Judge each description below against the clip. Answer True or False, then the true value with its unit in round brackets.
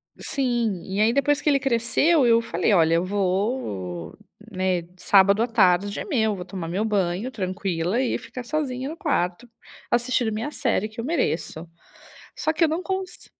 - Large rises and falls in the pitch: True (6.0 semitones)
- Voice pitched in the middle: False (220 Hz)